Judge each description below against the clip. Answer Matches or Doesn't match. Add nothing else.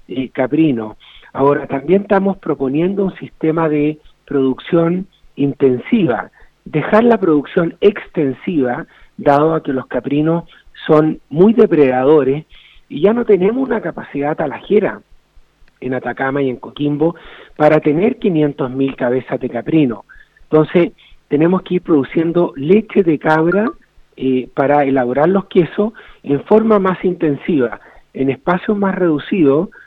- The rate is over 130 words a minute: Doesn't match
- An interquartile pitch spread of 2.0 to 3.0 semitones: Doesn't match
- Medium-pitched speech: Matches